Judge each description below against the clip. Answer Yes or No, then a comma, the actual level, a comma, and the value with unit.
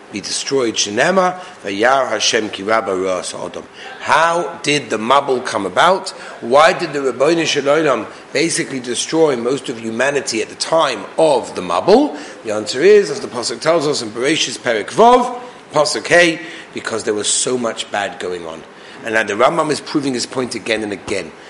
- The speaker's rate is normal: Yes, average, 175 wpm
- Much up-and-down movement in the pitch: Yes, wide, 8.4 semitones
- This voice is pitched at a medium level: Yes, medium, 150 Hz